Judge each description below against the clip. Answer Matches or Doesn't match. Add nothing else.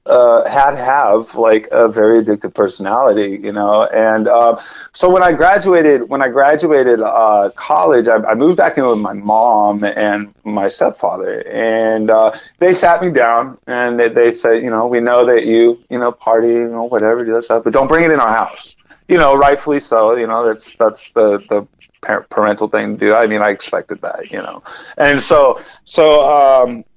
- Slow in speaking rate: Doesn't match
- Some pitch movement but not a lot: Matches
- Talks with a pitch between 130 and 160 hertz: Doesn't match